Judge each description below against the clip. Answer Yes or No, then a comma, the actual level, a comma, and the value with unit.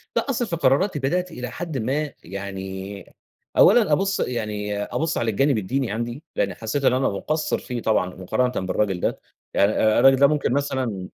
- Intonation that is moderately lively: No, wide, 6.1 semitones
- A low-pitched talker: Yes, low, 125 Hz